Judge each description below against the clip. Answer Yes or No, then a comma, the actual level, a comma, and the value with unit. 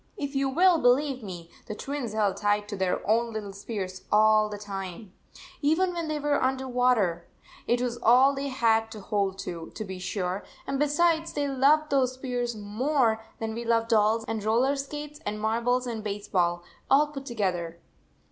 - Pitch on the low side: No, high, 230 Hz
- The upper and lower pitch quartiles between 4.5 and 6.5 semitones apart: Yes, average, 4.8 semitones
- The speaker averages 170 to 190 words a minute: Yes, average, 185 wpm